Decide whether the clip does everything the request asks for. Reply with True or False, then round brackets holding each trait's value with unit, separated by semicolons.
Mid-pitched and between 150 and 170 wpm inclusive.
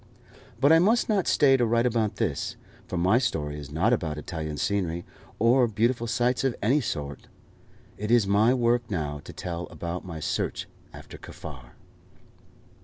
False (105 Hz; 165 wpm)